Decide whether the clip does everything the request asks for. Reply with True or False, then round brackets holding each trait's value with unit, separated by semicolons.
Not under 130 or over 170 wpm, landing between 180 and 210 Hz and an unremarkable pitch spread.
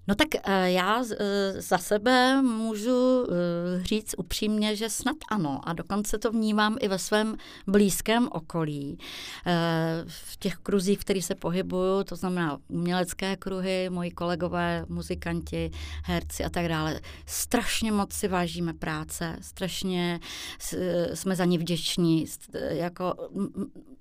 False (120 wpm; 185 Hz; 3.9 semitones)